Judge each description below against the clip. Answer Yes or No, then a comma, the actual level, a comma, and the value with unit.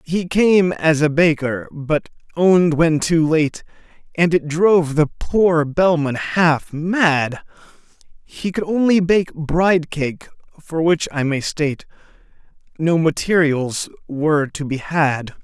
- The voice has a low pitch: No, medium, 160 Hz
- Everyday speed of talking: No, slow, 130 wpm